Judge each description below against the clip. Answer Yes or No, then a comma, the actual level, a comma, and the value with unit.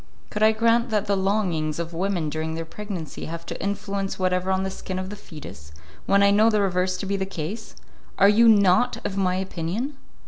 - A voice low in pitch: No, high, 190 Hz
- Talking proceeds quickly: Yes, fast, 210 wpm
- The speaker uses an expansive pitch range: No, average, 2.8 semitones